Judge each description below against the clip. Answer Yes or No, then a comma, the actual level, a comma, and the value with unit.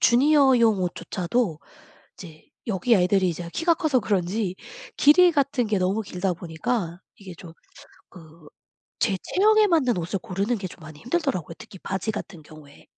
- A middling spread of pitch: No, wide, 6.1 semitones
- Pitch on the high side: Yes, high, 195 Hz